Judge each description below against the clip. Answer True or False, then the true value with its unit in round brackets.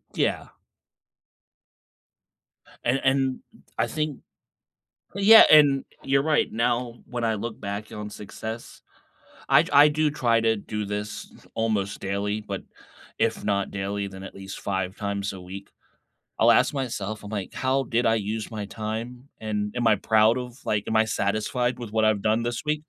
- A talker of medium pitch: False (110 Hz)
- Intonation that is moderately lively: True (3.2 semitones)